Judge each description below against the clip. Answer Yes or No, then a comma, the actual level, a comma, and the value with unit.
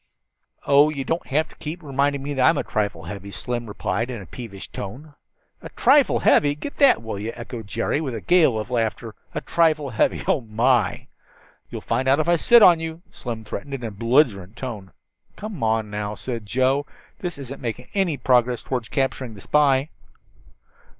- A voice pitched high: No, low, 130 Hz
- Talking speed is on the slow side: No, average, 185 wpm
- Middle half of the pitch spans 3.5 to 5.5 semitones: Yes, average, 4.8 semitones